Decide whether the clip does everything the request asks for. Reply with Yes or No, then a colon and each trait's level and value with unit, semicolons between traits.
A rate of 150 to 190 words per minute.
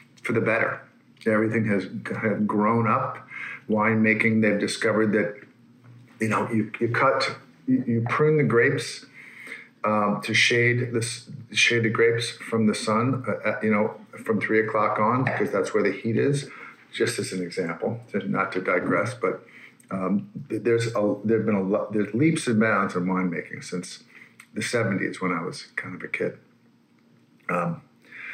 Yes: average, 170 wpm